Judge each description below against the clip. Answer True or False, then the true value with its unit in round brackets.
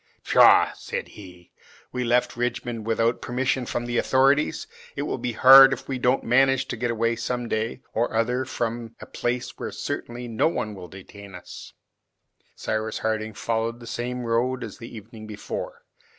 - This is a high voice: False (120 Hz)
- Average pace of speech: True (170 wpm)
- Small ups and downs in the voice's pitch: True (2.0 semitones)